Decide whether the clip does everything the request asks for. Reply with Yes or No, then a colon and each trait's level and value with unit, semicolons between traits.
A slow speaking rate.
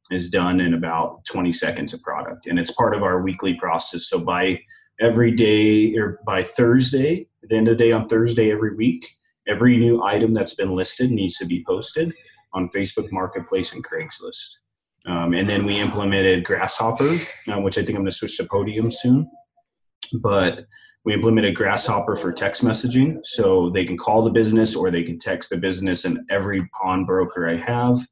No: average, 190 wpm